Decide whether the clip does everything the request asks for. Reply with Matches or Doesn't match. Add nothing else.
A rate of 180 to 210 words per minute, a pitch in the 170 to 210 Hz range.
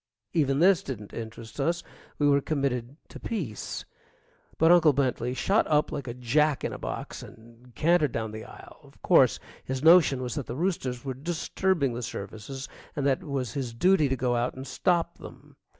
Doesn't match